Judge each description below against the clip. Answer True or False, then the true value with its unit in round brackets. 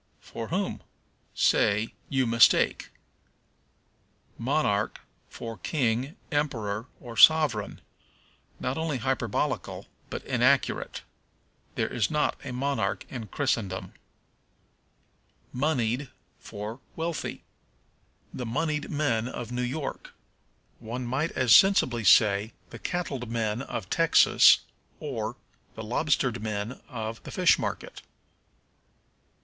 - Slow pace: True (100 wpm)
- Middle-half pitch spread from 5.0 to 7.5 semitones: False (4.4 semitones)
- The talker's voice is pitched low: True (125 Hz)